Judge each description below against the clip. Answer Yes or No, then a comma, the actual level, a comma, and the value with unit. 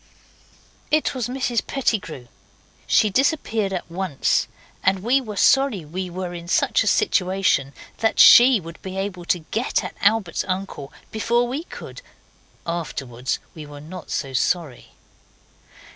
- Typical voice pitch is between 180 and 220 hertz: Yes, high, 190 Hz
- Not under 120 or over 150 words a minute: Yes, average, 140 wpm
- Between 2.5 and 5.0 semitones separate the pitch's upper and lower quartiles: No, wide, 5.6 semitones